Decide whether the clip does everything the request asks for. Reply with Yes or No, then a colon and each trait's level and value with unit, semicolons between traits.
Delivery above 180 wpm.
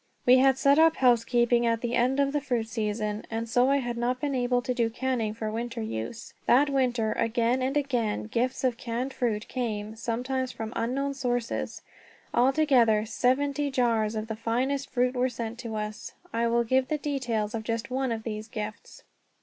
Yes: average, 190 wpm